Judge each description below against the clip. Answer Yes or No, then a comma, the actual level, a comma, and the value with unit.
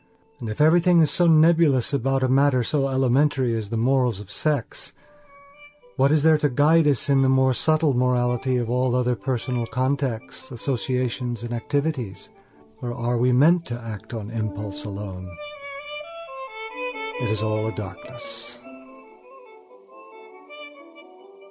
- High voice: No, low, 125 Hz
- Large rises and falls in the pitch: No, average, 3.4 semitones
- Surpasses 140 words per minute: No, slow, 135 wpm